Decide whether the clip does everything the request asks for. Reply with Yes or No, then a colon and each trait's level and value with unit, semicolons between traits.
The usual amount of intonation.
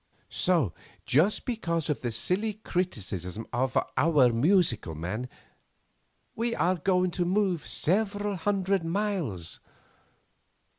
No: wide, 8.0 semitones